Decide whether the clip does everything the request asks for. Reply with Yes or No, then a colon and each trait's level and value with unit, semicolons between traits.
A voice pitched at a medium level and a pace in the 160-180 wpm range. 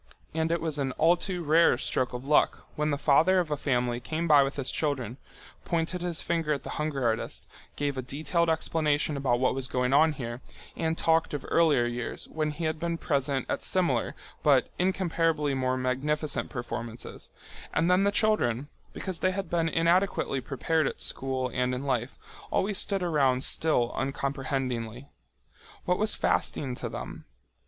Yes: medium, 145 Hz; average, 175 wpm